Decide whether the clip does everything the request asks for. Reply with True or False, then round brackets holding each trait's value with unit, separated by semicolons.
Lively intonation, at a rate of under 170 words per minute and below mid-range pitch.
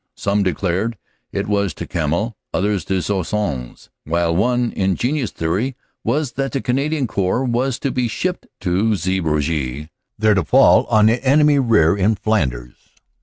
True (6.0 semitones; 155 wpm; 105 Hz)